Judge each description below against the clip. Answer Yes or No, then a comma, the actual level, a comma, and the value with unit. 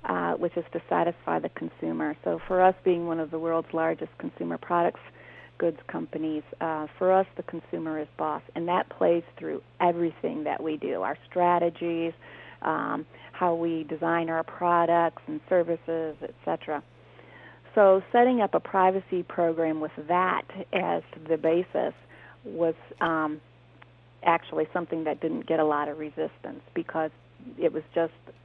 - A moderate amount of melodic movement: No, narrow, 2.0 semitones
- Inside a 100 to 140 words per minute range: No, average, 150 wpm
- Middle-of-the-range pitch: Yes, medium, 165 Hz